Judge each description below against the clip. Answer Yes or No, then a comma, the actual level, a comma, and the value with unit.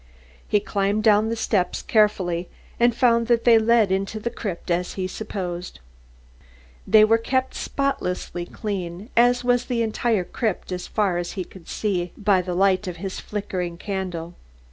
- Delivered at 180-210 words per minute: No, average, 165 wpm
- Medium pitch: No, high, 200 Hz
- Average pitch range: Yes, average, 3.9 semitones